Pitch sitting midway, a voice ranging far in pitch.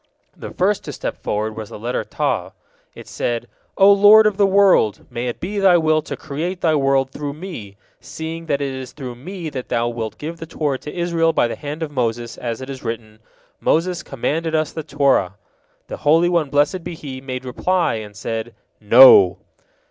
Yes: medium, 145 Hz; wide, 5.7 semitones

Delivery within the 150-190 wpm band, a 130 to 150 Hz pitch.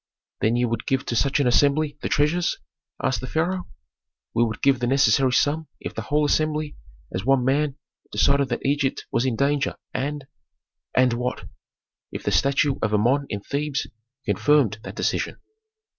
Yes: average, 175 wpm; medium, 140 Hz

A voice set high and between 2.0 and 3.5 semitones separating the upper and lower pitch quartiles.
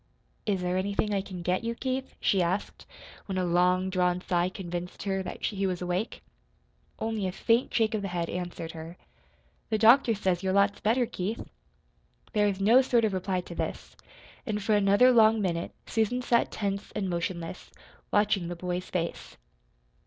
Yes: high, 195 Hz; average, 3.2 semitones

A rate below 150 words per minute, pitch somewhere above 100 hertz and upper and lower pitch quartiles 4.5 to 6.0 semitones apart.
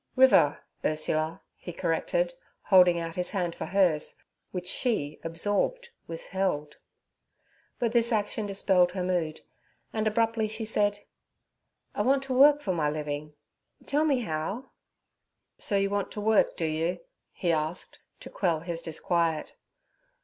Yes: average, 140 wpm; medium, 185 Hz; average, 5.2 semitones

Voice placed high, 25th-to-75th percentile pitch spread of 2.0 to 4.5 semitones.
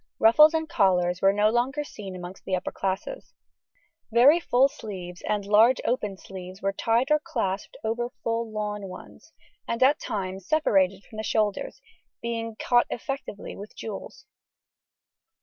Yes: high, 215 Hz; average, 3.9 semitones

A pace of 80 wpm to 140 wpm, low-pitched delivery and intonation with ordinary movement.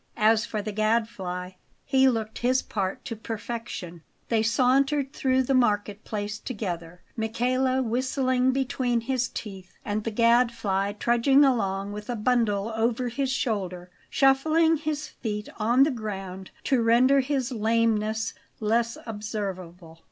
No: slow, 135 wpm; high, 230 Hz; average, 3.6 semitones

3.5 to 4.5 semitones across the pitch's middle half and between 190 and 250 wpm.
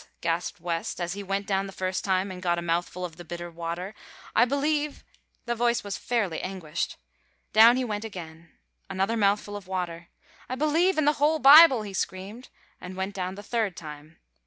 No: average, 5.1 semitones; average, 195 wpm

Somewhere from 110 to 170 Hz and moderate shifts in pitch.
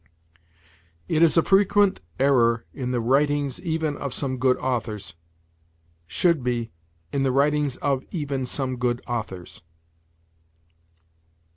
Yes: low, 135 Hz; average, 3.3 semitones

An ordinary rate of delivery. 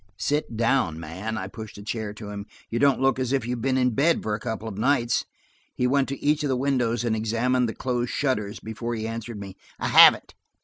No: fast, 235 wpm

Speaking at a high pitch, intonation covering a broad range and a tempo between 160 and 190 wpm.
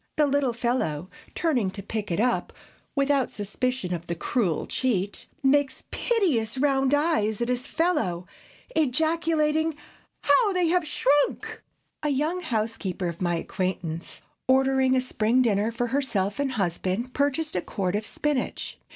No: very high, 255 Hz; wide, 6.3 semitones; average, 145 wpm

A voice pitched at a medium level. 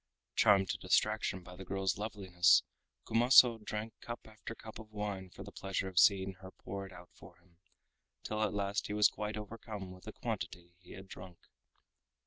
No: low, 100 Hz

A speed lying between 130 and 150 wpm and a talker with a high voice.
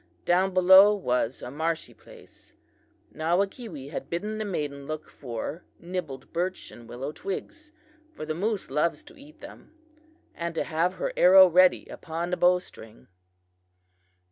No: average, 145 wpm; medium, 175 Hz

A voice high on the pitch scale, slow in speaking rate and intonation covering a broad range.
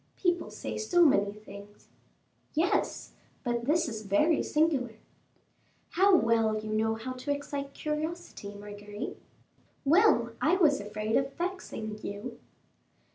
Yes: very high, 250 Hz; slow, 125 wpm; wide, 6.9 semitones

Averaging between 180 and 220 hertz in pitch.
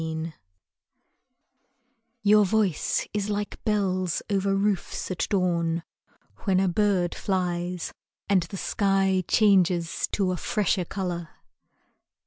Yes: high, 190 Hz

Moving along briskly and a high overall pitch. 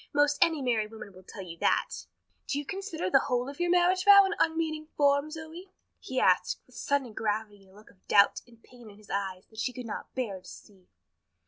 Yes: fast, 225 wpm; very high, 250 Hz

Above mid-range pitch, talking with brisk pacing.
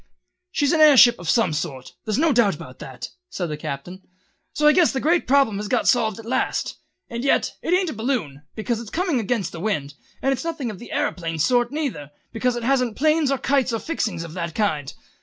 Yes: high, 235 Hz; fast, 230 wpm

